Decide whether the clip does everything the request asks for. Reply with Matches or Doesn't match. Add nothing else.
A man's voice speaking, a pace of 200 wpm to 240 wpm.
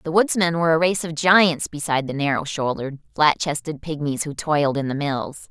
Doesn't match